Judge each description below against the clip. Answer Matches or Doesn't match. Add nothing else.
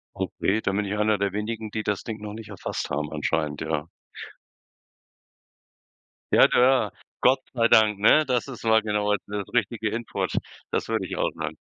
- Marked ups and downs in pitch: Doesn't match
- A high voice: Doesn't match